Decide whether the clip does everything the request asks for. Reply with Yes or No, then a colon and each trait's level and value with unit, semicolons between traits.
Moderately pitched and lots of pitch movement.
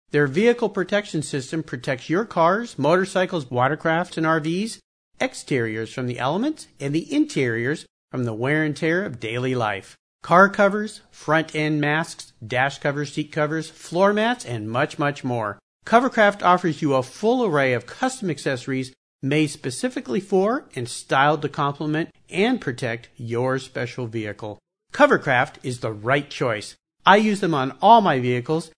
Yes: medium, 155 Hz; wide, 6.1 semitones